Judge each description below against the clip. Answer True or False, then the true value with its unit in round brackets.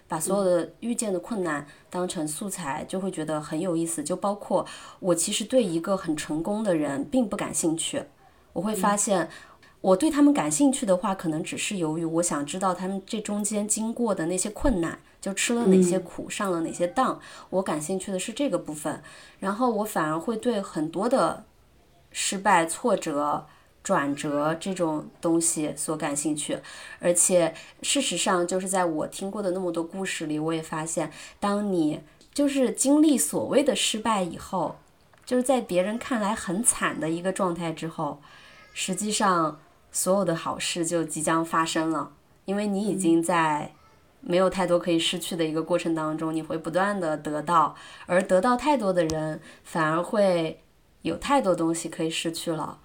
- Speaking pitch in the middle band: True (180 Hz)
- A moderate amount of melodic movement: True (3.9 semitones)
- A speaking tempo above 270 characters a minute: False (265 characters per minute)